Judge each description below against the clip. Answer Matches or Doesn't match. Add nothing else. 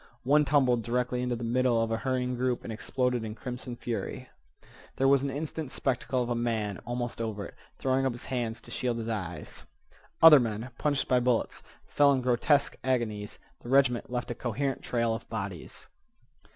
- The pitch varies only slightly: Matches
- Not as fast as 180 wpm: Doesn't match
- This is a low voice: Matches